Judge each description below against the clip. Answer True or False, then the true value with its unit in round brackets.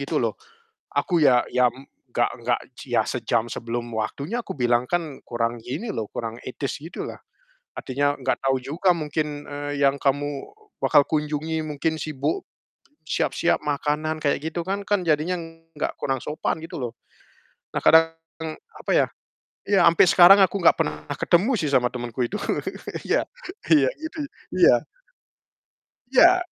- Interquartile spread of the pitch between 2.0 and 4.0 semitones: False (4.5 semitones)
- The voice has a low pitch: False (150 Hz)